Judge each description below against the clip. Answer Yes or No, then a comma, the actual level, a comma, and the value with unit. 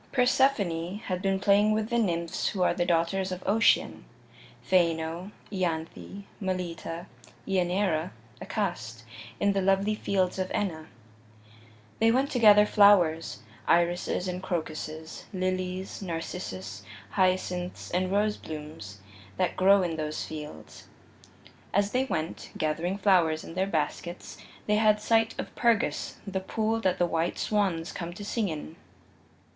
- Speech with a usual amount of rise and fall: Yes, average, 3.5 semitones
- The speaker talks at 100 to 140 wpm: Yes, slow, 135 wpm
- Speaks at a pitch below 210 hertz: Yes, medium, 185 Hz